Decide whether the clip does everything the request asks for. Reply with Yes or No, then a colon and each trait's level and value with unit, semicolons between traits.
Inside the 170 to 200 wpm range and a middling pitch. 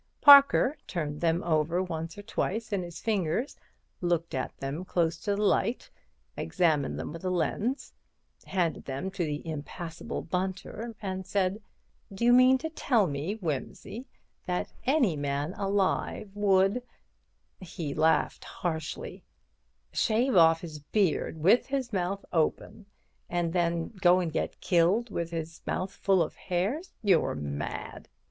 No: average, 140 wpm; medium, 180 Hz